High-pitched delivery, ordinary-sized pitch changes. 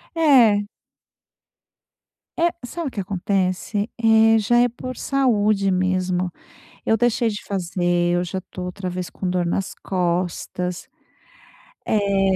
Yes: high, 195 Hz; average, 3.6 semitones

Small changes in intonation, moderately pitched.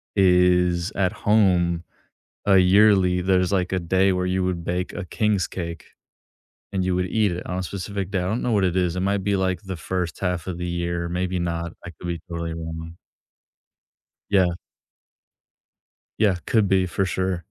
No: narrow, 1.7 semitones; very low, 90 Hz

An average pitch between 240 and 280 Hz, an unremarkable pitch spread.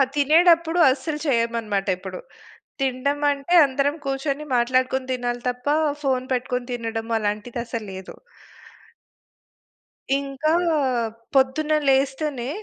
Yes: very high, 260 Hz; average, 3.1 semitones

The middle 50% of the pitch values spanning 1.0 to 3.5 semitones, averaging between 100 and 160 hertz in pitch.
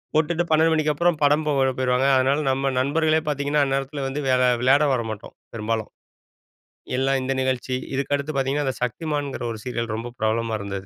Yes: average, 2.9 semitones; low, 135 Hz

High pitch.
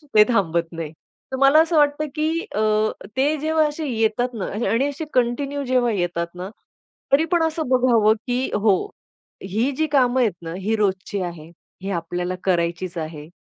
Yes: high, 225 Hz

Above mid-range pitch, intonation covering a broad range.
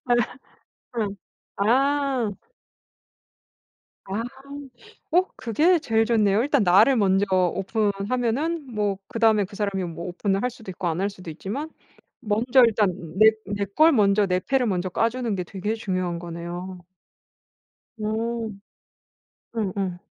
No: high, 210 Hz; average, 3.6 semitones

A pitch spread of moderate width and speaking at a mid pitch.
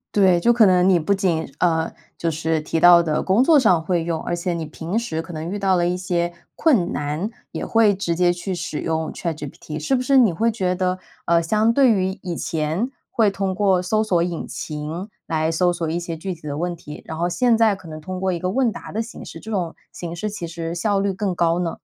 Yes: average, 3.3 semitones; medium, 175 Hz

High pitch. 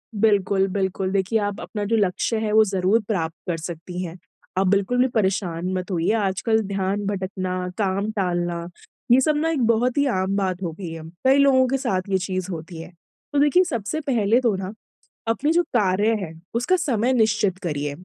Yes: high, 200 Hz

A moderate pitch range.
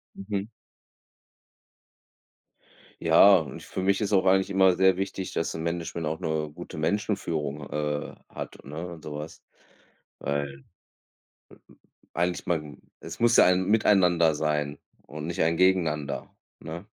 Yes: average, 3.8 semitones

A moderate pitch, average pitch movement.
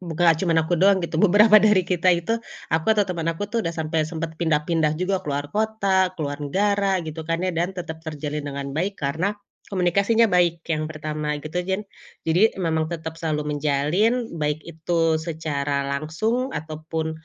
Yes: medium, 165 Hz; average, 3.4 semitones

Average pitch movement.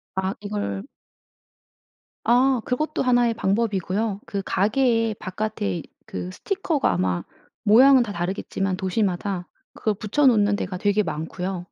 Yes: average, 4.0 semitones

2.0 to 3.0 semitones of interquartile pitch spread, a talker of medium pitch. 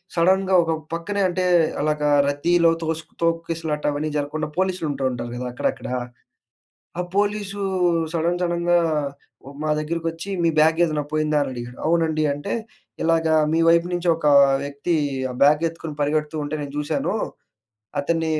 Yes: narrow, 2.4 semitones; medium, 160 Hz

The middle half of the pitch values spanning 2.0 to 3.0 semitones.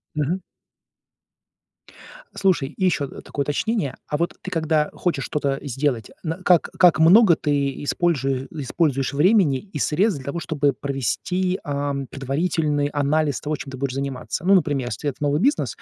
No: average, 3.7 semitones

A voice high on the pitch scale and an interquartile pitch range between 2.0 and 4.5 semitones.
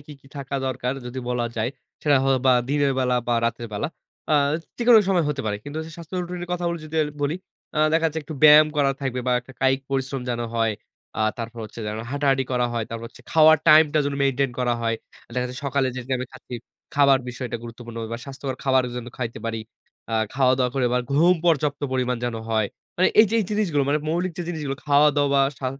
No: low, 135 Hz; average, 3.4 semitones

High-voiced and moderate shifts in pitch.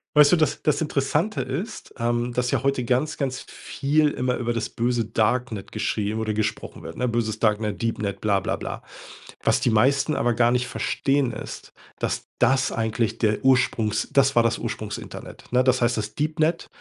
No: low, 125 Hz; average, 3.6 semitones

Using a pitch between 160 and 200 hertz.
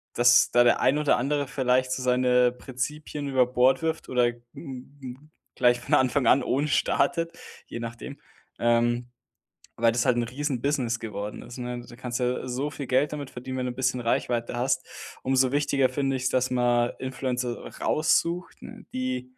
No: low, 125 Hz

